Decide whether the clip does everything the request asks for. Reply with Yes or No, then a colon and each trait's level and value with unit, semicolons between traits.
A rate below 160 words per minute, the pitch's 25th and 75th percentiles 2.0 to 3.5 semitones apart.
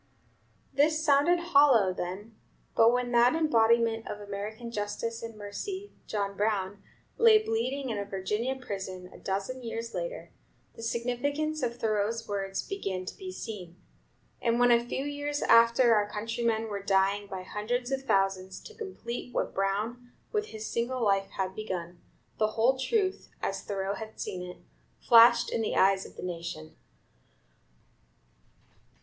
No: average, 150 wpm; average, 4.1 semitones